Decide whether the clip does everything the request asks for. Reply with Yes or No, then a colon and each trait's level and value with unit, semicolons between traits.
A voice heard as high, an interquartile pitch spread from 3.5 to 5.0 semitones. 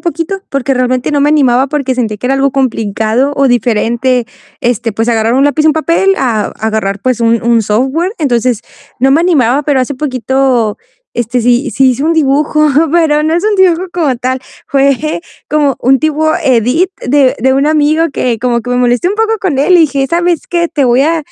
Yes: very high, 270 Hz; average, 4.1 semitones